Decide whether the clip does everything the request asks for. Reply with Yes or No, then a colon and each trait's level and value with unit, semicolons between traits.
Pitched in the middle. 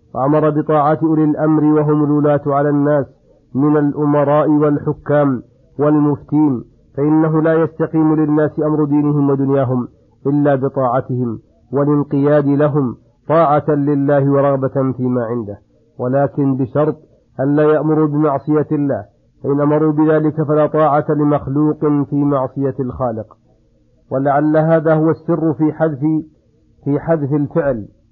Yes: medium, 145 Hz